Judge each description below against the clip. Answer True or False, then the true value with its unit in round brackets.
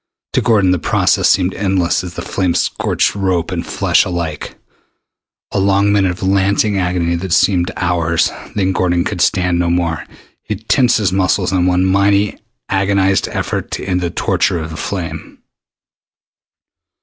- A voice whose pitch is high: False (95 Hz)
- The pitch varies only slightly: True (2.0 semitones)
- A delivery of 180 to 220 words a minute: False (160 wpm)